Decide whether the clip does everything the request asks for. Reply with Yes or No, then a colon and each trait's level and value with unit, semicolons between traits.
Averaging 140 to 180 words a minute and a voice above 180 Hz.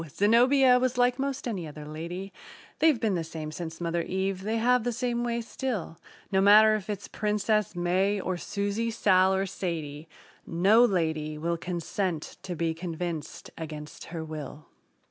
Yes: average, 165 wpm; high, 190 Hz